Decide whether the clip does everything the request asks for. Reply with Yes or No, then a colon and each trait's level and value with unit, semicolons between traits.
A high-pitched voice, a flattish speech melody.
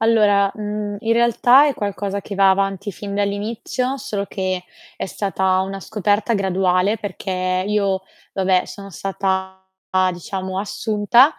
Yes: high, 200 Hz; narrow, 1.8 semitones